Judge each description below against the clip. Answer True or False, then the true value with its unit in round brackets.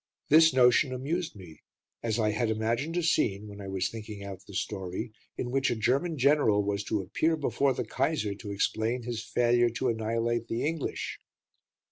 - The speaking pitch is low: True (115 Hz)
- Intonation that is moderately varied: True (4.1 semitones)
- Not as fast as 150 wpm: False (180 wpm)